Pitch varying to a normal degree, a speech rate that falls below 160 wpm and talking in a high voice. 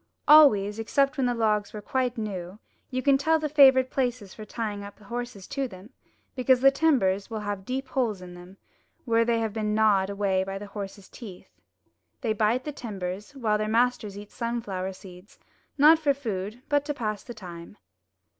No: average, 4.4 semitones; average, 185 wpm; high, 220 Hz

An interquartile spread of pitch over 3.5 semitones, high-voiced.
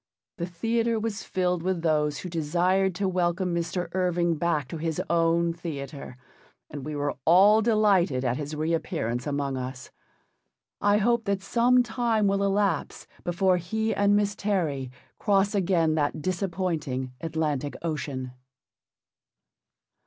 No: average, 4.7 semitones; medium, 175 Hz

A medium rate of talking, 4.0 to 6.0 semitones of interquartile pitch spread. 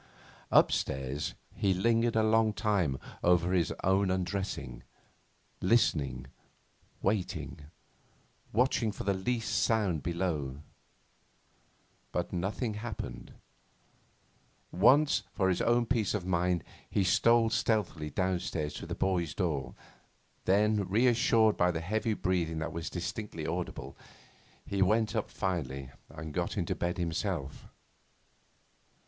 No: slow, 115 wpm; average, 4.6 semitones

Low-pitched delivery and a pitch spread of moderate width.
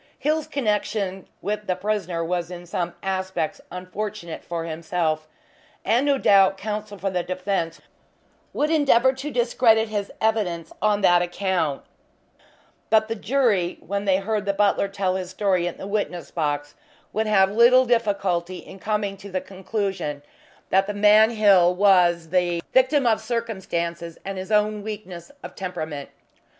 No: high, 195 Hz; average, 3.3 semitones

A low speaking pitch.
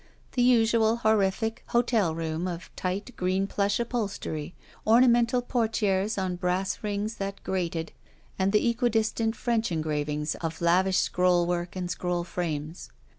No: high, 190 Hz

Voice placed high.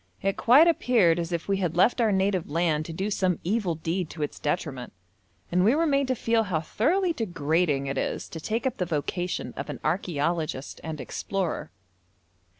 No: medium, 180 Hz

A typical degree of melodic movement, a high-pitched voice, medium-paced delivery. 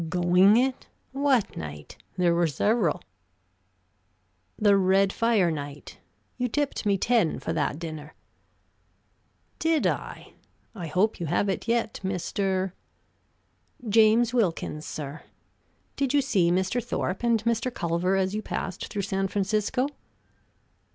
No: average, 4.9 semitones; high, 195 Hz; slow, 130 wpm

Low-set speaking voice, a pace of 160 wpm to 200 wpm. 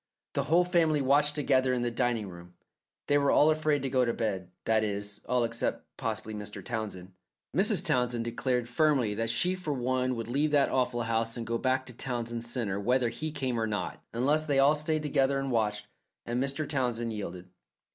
Yes: low, 125 Hz; average, 195 wpm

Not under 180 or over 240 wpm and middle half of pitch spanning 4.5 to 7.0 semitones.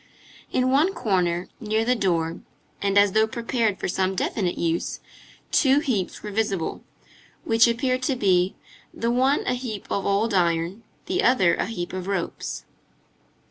No: average, 155 wpm; average, 4.9 semitones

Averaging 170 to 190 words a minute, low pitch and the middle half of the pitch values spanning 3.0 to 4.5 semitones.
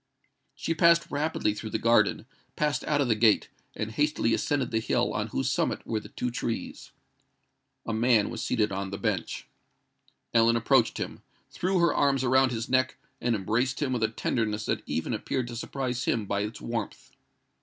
Yes: average, 185 wpm; low, 115 Hz; average, 3.4 semitones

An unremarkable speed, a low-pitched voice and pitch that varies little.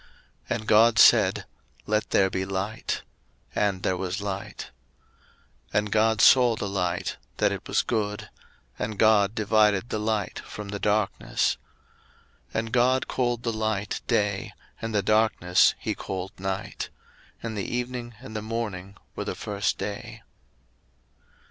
Yes: average, 150 wpm; low, 105 Hz; narrow, 2.2 semitones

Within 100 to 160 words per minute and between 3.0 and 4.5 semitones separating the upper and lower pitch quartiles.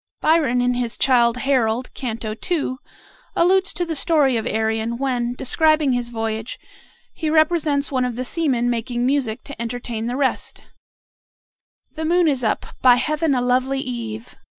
Yes: average, 155 wpm; average, 3.8 semitones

